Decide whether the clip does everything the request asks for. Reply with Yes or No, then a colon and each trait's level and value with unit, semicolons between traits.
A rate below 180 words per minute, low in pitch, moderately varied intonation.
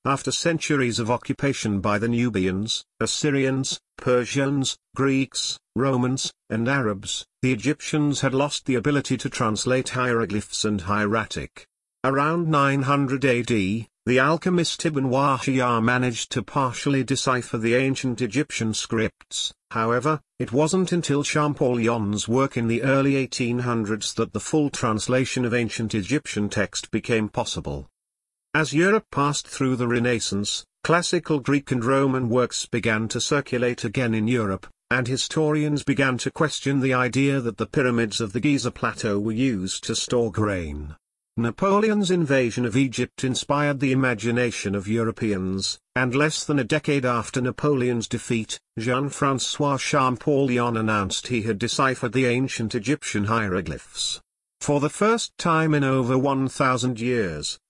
Yes: slow, 135 wpm; low, 125 Hz; average, 3.4 semitones